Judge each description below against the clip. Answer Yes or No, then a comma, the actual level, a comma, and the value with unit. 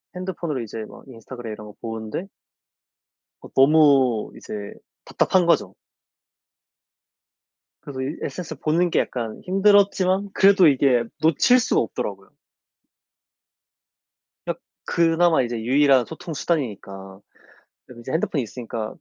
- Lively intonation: Yes, wide, 6.7 semitones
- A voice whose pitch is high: No, medium, 140 Hz